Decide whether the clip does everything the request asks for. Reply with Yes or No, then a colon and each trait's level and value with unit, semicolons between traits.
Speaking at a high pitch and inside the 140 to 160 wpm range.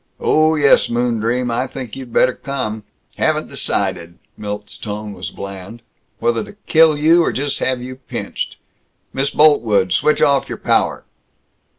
No: low, 125 Hz; average, 150 wpm